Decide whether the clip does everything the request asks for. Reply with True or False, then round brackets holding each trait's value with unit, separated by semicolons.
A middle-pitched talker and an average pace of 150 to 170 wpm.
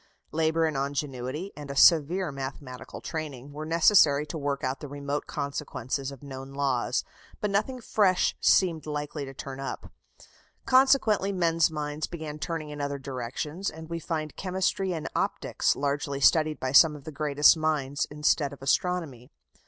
True (150 Hz; 160 wpm)